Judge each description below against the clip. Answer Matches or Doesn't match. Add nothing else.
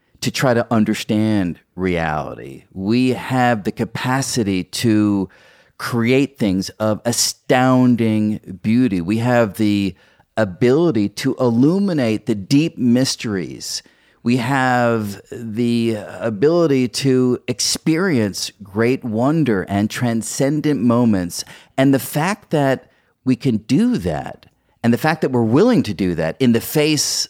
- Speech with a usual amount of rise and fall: Matches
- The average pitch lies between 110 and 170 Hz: Matches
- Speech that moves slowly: Matches